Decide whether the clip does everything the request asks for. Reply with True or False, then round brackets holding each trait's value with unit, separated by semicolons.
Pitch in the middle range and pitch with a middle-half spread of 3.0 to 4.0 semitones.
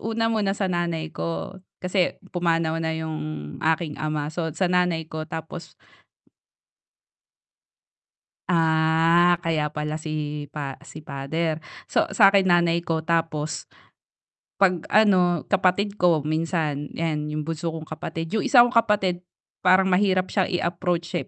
False (165 Hz; 2.6 semitones)